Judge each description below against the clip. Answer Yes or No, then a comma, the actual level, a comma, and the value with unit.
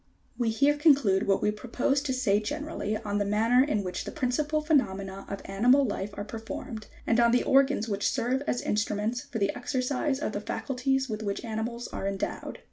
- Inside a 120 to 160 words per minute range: No, average, 200 wpm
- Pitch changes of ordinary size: Yes, average, 4.5 semitones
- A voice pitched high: Yes, high, 235 Hz